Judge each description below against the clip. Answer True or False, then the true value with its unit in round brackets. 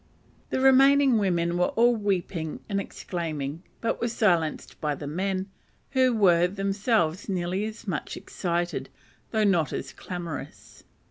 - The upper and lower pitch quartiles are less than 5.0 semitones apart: True (4.2 semitones)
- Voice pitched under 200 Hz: True (190 Hz)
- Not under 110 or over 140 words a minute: True (135 wpm)